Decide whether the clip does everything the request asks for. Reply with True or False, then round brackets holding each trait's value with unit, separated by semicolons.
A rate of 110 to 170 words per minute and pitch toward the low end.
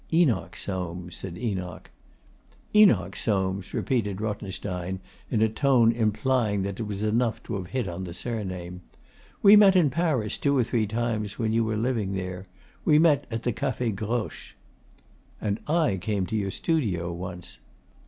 True (160 wpm; 105 Hz)